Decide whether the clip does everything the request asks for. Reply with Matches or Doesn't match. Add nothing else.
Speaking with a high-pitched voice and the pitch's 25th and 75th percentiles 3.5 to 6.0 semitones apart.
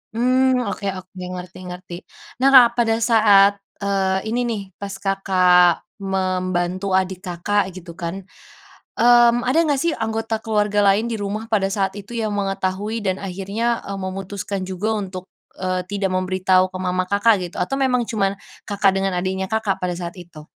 Doesn't match